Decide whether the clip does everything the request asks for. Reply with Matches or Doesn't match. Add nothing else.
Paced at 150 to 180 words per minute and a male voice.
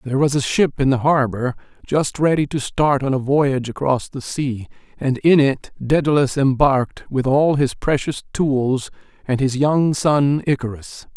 Matches